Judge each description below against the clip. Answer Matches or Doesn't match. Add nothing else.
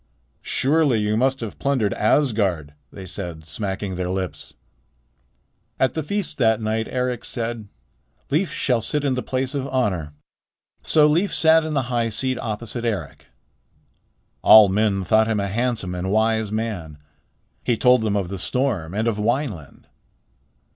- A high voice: Doesn't match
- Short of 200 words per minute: Matches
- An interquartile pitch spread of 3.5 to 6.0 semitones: Matches